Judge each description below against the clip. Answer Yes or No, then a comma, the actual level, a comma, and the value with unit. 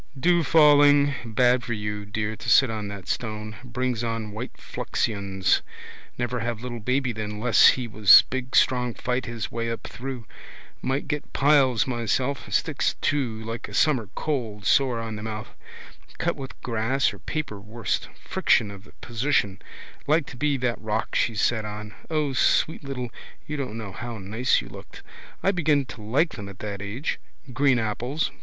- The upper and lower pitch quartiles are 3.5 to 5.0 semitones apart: Yes, average, 3.9 semitones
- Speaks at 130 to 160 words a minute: No, average, 175 wpm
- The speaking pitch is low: Yes, low, 120 Hz